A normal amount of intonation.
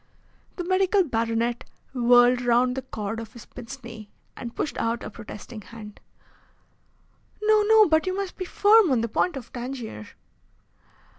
No: wide, 7.5 semitones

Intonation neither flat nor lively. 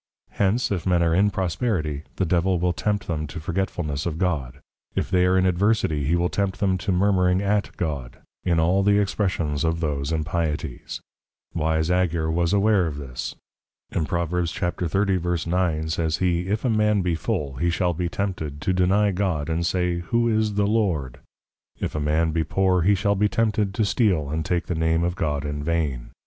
Yes: average, 3.4 semitones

